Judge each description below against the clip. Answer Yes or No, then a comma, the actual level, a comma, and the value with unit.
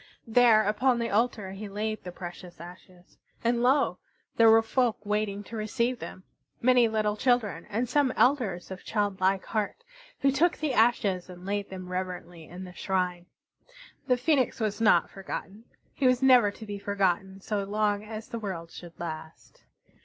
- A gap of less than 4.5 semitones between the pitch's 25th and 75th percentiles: Yes, average, 3.9 semitones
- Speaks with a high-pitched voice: Yes, high, 210 Hz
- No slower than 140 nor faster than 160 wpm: No, average, 170 wpm